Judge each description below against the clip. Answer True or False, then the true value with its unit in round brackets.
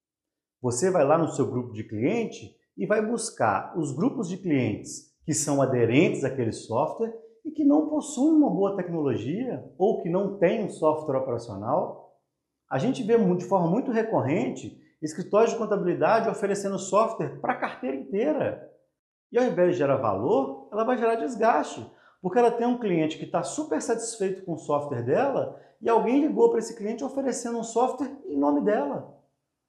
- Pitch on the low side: False (200 Hz)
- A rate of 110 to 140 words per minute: False (170 wpm)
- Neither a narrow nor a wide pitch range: False (6.5 semitones)